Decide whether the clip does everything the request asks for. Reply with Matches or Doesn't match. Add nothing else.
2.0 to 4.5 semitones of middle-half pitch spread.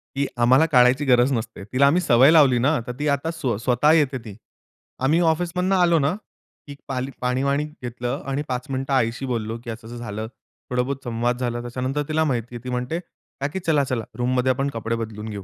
Matches